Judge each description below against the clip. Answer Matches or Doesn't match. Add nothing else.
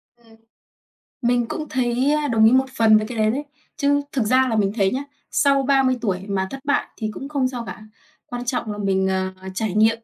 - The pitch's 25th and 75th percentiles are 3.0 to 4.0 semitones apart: Matches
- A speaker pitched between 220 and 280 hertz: Matches